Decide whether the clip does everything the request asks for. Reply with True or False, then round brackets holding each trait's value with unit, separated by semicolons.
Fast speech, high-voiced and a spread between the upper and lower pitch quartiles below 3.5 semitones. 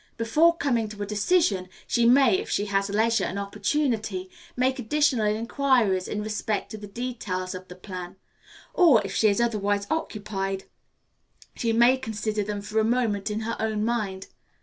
False (170 wpm; 215 Hz; 3.1 semitones)